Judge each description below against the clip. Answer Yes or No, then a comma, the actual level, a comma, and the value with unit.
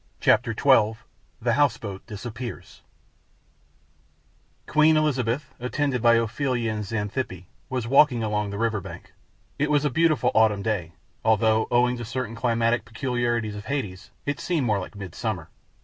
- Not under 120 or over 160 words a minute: Yes, average, 145 wpm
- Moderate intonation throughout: Yes, average, 3.3 semitones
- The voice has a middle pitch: No, low, 115 Hz